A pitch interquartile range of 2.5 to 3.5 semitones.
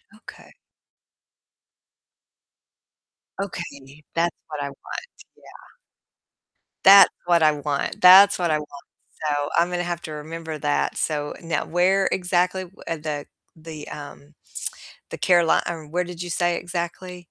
Yes: average, 2.8 semitones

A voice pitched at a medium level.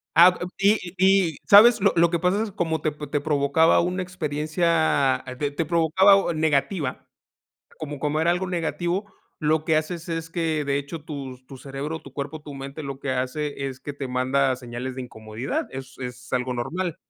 Yes: medium, 150 Hz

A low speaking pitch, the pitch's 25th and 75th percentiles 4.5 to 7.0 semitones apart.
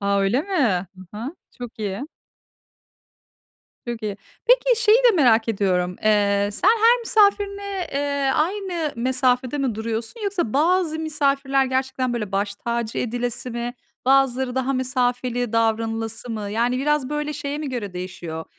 No: very high, 255 Hz; average, 5.0 semitones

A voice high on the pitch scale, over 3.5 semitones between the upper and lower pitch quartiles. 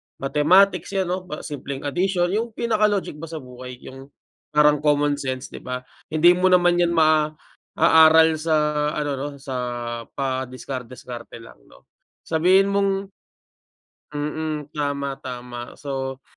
No: medium, 150 Hz; average, 4.7 semitones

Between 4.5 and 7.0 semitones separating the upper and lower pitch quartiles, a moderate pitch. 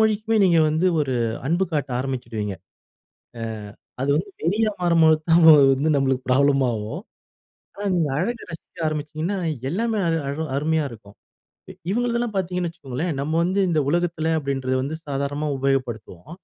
Yes: average, 4.9 semitones; medium, 155 Hz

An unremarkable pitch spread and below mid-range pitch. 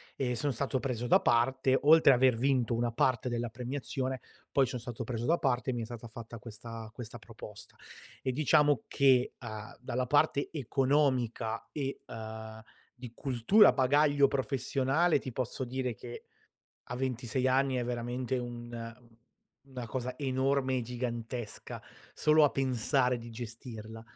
No: narrow, 2.2 semitones; low, 125 Hz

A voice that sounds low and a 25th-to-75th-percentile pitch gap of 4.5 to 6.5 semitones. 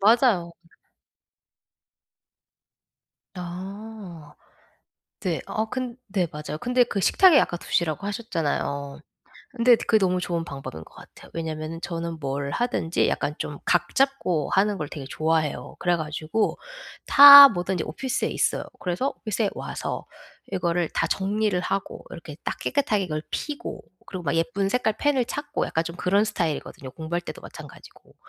No: medium, 180 Hz; wide, 5.4 semitones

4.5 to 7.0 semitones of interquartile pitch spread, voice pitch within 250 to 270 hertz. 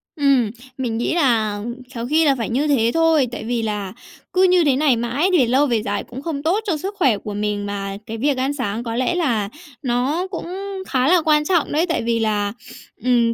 Yes: average, 5.0 semitones; very high, 255 Hz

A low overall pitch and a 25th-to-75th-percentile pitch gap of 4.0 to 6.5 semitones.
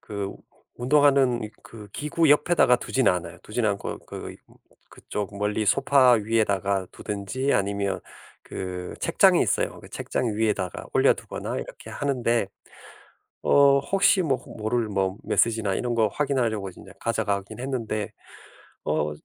Yes: low, 110 Hz; average, 4.7 semitones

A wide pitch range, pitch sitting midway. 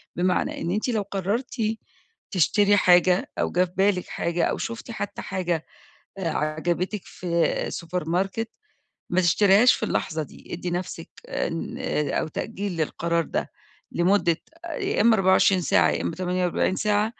No: average, 3.0 semitones; medium, 180 Hz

